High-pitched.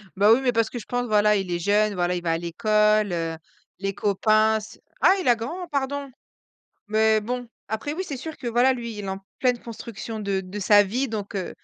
Yes: high, 215 Hz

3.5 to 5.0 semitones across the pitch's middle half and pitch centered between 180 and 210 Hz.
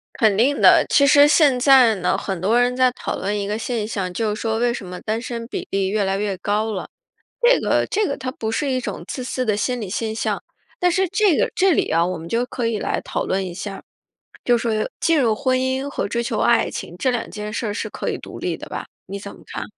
No: average, 4.1 semitones; high, 230 Hz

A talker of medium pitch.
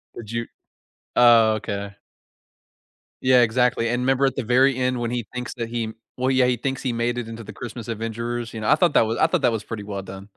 No: low, 120 Hz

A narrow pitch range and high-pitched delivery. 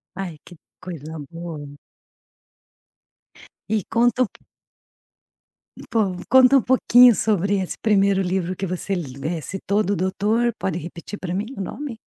No: average, 4.0 semitones; high, 195 Hz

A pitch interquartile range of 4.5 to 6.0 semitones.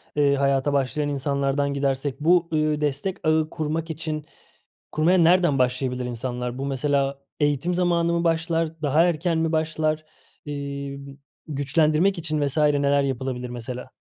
No: average, 2.7 semitones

